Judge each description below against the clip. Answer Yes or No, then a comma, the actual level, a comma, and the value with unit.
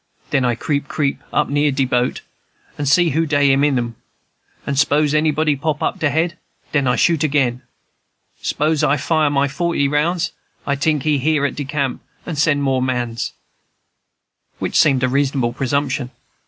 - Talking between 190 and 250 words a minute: No, average, 170 wpm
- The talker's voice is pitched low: No, medium, 145 Hz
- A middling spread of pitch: No, narrow, 2.3 semitones